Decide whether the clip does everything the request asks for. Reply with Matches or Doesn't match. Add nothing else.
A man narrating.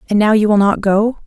Doesn't match